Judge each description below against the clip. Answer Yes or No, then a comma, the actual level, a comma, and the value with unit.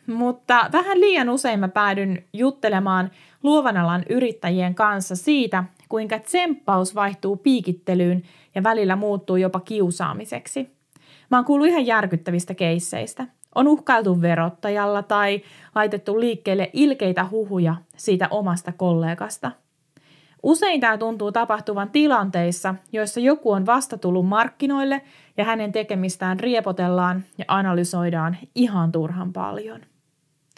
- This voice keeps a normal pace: Yes, average, 110 wpm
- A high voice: Yes, high, 200 Hz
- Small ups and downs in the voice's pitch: No, average, 4.6 semitones